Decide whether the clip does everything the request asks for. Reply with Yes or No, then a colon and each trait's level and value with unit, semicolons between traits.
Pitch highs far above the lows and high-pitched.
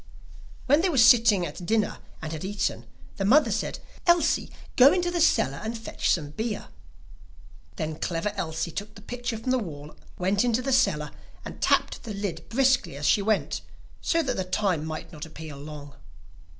Yes: wide, 7.5 semitones; high, 205 Hz